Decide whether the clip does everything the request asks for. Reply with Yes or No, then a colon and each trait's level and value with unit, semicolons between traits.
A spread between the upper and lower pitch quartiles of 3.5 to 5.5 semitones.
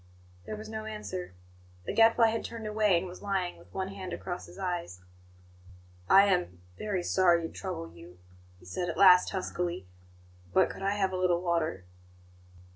No: average, 2.7 semitones